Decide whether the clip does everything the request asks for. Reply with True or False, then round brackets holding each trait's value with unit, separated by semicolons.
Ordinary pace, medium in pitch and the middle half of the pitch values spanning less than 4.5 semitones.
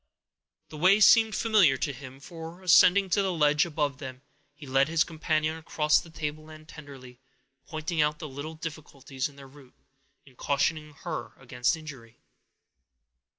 True (150 wpm; 150 Hz; 2.8 semitones)